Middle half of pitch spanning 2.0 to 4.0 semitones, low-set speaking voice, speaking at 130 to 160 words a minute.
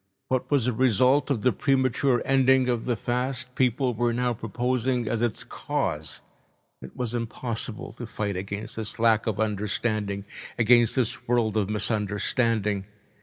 Yes: average, 2.8 semitones; low, 115 Hz; average, 150 wpm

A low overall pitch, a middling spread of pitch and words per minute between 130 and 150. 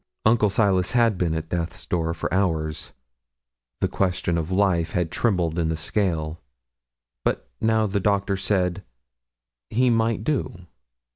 Yes: very low, 95 Hz; average, 3.9 semitones; average, 140 wpm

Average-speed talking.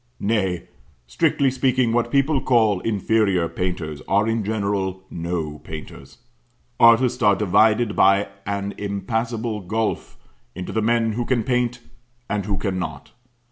No: slow, 130 wpm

